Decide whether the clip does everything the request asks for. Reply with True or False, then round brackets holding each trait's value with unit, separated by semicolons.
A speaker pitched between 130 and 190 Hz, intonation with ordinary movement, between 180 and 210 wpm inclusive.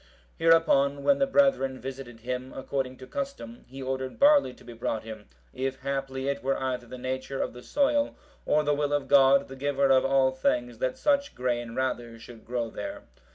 False (135 Hz; 2.2 semitones; 195 wpm)